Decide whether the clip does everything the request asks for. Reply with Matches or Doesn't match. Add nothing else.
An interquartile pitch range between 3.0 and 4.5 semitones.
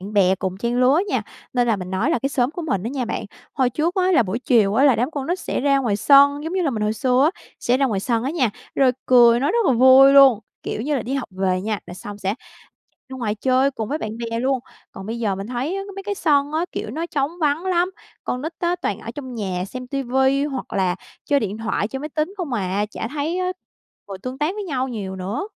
Doesn't match